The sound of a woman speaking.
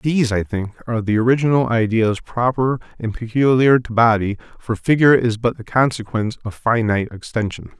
No: male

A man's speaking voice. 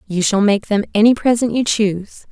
No: female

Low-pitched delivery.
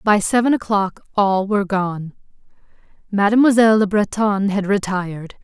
No: high, 200 Hz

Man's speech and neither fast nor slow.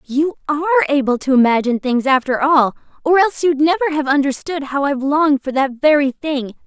No: female; average, 190 wpm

